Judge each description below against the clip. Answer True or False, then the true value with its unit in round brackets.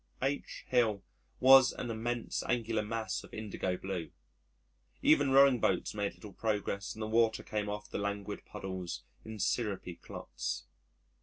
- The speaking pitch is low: True (110 Hz)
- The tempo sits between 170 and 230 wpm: False (145 wpm)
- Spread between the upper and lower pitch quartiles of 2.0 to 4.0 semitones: True (3.0 semitones)